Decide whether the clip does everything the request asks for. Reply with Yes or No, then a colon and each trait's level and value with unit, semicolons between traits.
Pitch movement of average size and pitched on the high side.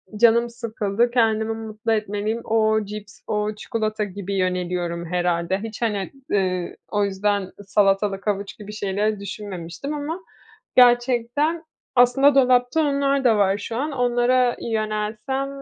Yes: average, 3.3 semitones; high, 215 Hz